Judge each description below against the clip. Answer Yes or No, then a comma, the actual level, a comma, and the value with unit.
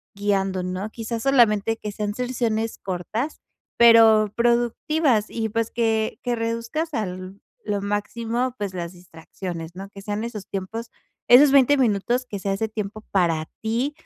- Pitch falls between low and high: No, high, 220 Hz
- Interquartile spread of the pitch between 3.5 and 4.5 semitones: No, average, 3.1 semitones